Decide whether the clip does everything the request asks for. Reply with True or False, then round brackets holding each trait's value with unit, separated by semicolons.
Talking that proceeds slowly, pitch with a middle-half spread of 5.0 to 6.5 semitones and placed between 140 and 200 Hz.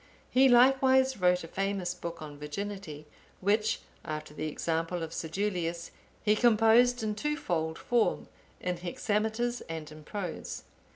True (130 wpm; 5.3 semitones; 190 Hz)